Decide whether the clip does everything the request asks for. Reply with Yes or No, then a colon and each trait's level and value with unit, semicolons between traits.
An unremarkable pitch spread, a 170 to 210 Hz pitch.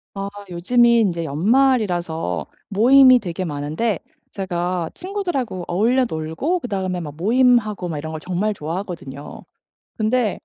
No: wide, 6.2 semitones; high, 190 Hz